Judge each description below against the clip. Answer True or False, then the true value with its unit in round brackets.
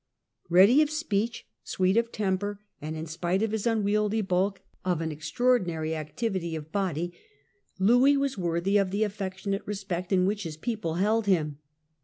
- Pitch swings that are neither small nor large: True (3.9 semitones)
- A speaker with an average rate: True (160 wpm)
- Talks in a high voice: True (195 Hz)